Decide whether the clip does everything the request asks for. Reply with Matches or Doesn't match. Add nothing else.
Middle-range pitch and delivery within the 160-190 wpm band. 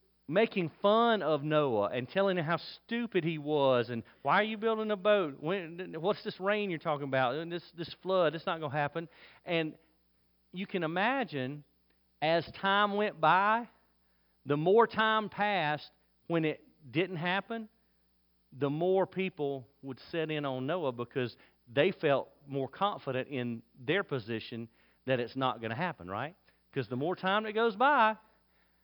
Matches